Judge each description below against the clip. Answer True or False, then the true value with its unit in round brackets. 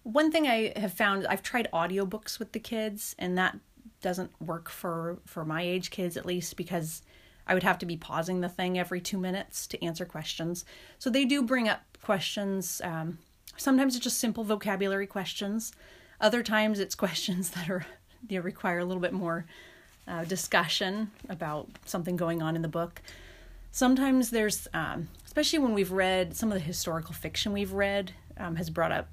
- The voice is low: False (185 Hz)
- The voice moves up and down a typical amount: True (3.8 semitones)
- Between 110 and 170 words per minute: False (185 wpm)